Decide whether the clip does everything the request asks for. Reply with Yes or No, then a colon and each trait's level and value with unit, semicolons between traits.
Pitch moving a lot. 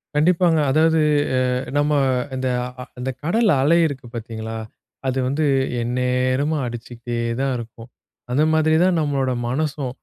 No: average, 4.0 semitones